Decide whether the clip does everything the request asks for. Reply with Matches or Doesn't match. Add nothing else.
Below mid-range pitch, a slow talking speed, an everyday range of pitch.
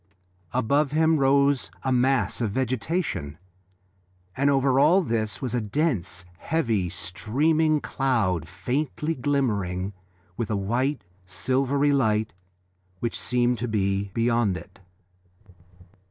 Matches